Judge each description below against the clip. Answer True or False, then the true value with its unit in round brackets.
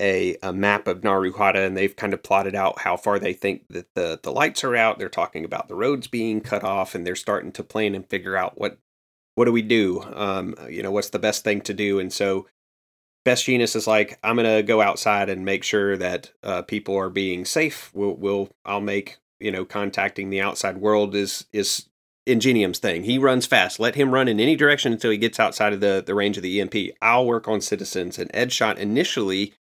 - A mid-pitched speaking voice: False (100 Hz)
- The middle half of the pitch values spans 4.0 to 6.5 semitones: False (2.5 semitones)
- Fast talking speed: True (225 wpm)